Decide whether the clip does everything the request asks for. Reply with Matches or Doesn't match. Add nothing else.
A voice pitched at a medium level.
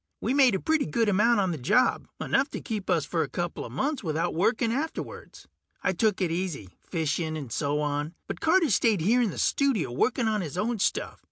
Doesn't match